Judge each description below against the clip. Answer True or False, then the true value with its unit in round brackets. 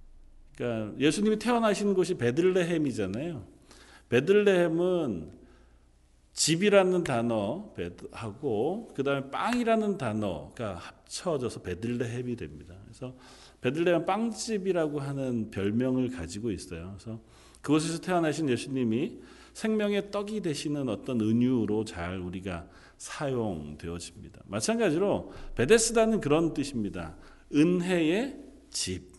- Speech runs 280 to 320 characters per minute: True (290 characters per minute)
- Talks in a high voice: False (130 Hz)